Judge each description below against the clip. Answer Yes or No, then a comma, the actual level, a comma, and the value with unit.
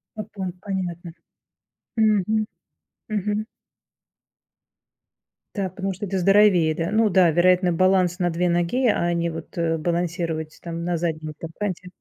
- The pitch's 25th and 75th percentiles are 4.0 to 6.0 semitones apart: No, average, 2.7 semitones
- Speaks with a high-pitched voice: No, medium, 180 Hz